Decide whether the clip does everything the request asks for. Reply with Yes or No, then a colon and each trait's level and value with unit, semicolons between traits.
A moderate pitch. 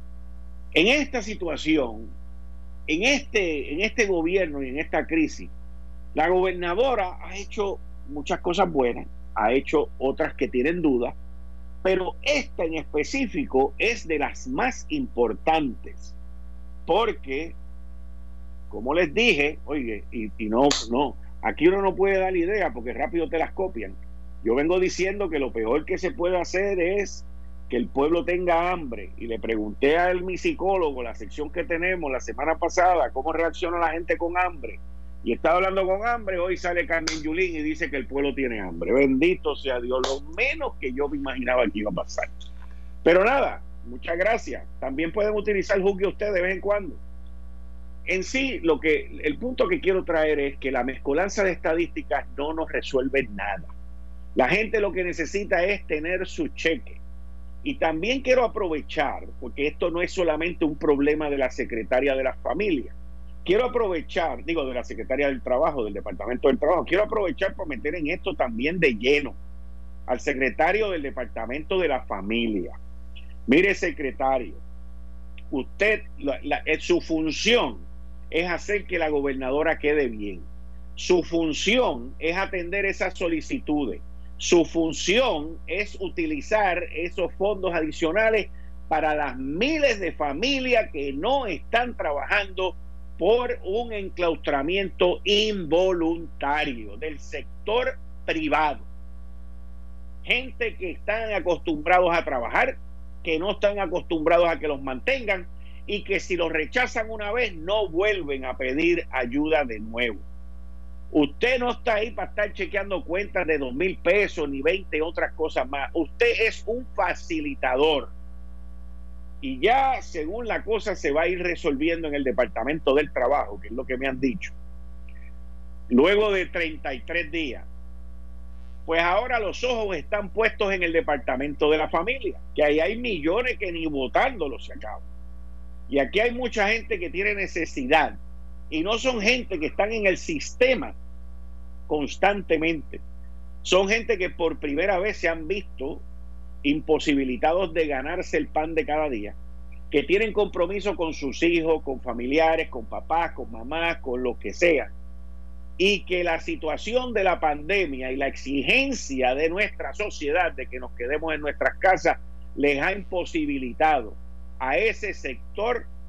Yes: medium, 155 Hz